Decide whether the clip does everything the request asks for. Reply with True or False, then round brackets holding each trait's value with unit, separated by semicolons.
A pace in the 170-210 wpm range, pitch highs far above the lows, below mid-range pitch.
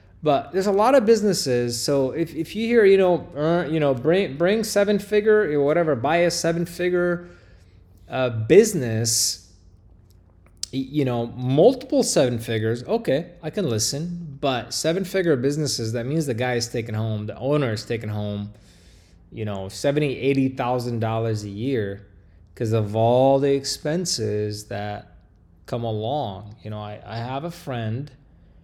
False (155 wpm; 7.3 semitones; 125 Hz)